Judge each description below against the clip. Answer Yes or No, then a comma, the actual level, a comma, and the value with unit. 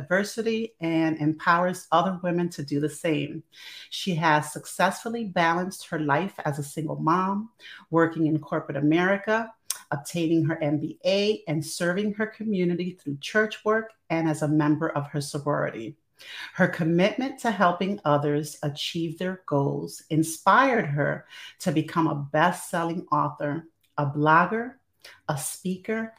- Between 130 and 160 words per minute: Yes, slow, 135 wpm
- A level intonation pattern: No, average, 3.9 semitones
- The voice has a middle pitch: Yes, medium, 165 Hz